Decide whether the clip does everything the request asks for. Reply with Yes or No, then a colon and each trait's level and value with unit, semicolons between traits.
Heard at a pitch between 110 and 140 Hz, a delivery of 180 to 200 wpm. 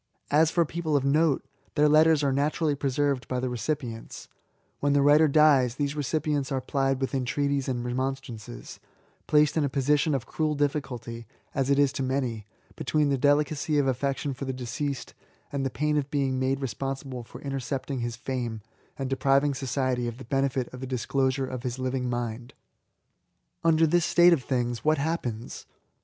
Yes: low, 135 Hz; average, 185 wpm